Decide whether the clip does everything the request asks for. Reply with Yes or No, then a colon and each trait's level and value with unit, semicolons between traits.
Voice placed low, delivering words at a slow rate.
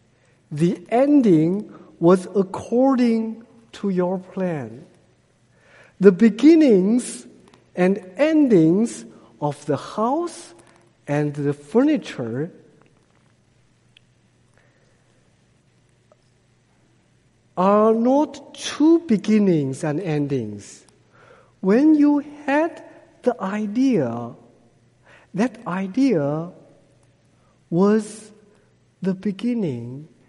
No: high, 190 Hz; slow, 65 wpm